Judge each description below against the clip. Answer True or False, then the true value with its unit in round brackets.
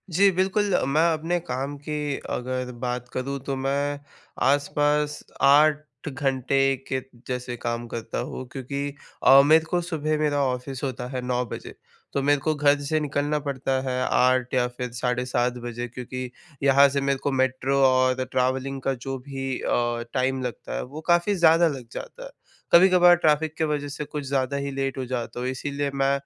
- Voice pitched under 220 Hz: True (135 Hz)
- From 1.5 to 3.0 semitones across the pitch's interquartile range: True (2.5 semitones)